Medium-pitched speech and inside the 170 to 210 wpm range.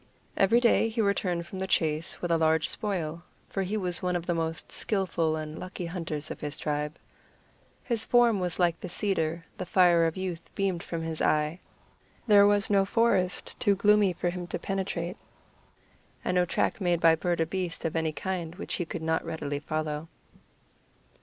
Yes: medium, 175 Hz; average, 185 wpm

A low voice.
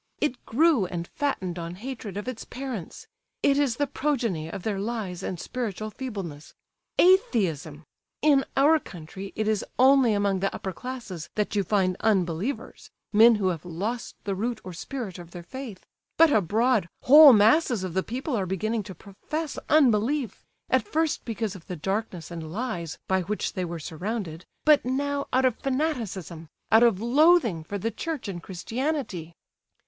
No: high, 215 Hz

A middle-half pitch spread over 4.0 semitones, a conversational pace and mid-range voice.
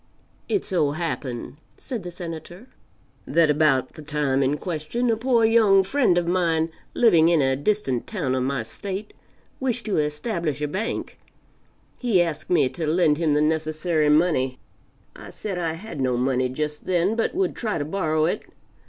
Yes: average, 4.7 semitones; average, 170 wpm; medium, 165 Hz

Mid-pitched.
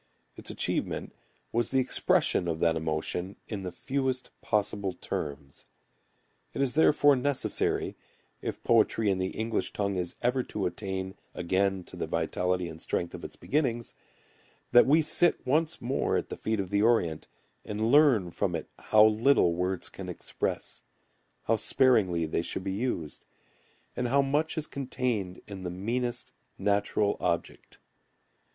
No: low, 105 Hz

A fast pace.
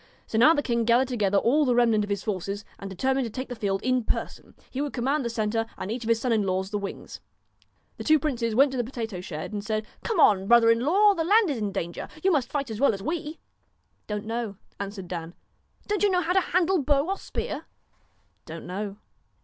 Yes: fast, 240 wpm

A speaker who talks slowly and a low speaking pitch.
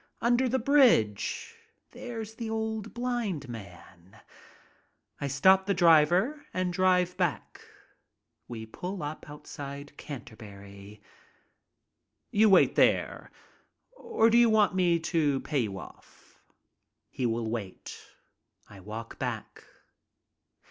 No: slow, 115 wpm; medium, 170 Hz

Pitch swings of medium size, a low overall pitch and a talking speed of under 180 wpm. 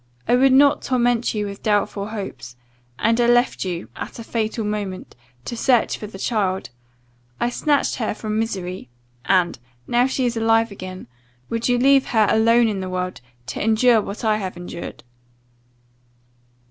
No: average, 3.8 semitones; high, 220 Hz; average, 165 wpm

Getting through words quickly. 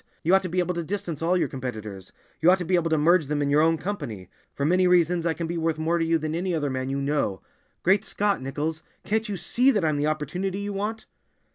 Yes: fast, 260 wpm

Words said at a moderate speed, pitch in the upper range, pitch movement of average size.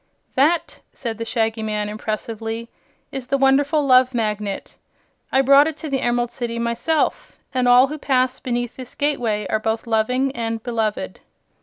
Yes: average, 160 wpm; high, 240 Hz; average, 3.2 semitones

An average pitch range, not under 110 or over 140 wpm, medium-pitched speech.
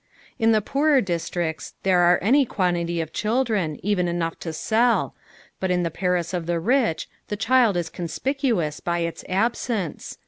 No: average, 4.9 semitones; average, 165 wpm; medium, 180 Hz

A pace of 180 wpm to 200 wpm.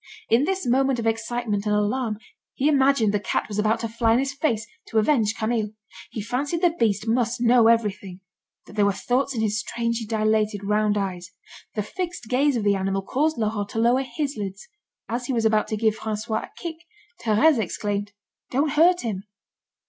Yes: average, 195 wpm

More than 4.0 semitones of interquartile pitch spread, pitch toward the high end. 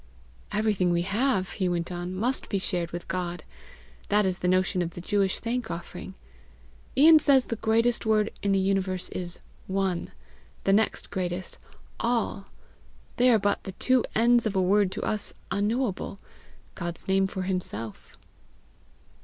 No: average, 3.3 semitones; high, 195 Hz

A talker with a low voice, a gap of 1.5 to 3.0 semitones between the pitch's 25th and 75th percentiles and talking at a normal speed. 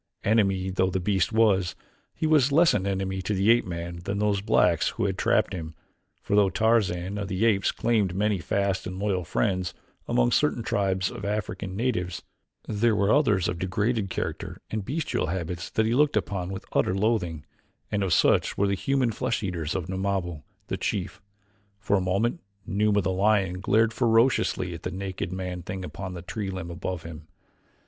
Yes: very low, 95 Hz; average, 2.7 semitones; average, 185 wpm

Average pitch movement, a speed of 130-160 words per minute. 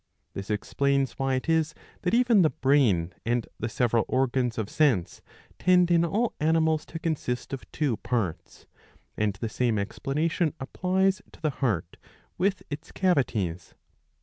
No: wide, 6.3 semitones; average, 150 wpm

